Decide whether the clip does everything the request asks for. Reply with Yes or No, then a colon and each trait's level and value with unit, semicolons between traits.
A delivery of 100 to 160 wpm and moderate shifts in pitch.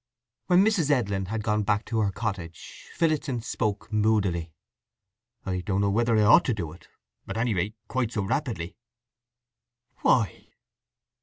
Yes: average, 145 wpm; average, 3.6 semitones